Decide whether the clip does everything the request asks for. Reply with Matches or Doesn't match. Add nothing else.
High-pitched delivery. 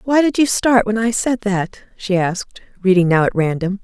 Matches